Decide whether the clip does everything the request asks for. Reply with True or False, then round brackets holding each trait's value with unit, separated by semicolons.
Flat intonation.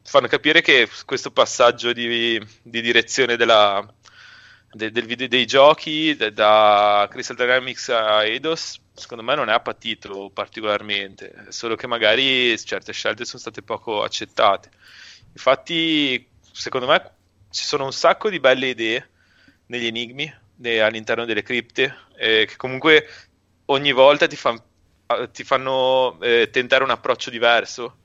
False (3.6 semitones)